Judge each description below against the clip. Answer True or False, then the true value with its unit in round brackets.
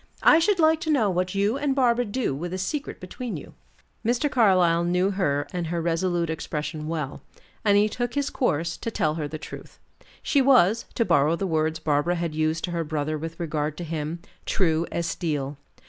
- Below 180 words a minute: False (200 wpm)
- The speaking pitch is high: False (175 Hz)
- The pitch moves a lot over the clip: True (5.9 semitones)